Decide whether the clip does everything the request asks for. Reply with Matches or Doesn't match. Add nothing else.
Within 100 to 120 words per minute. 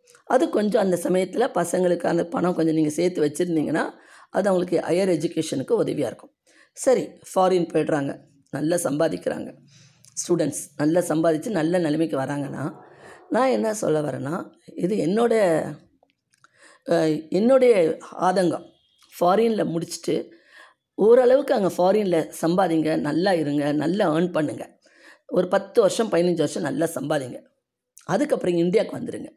Matches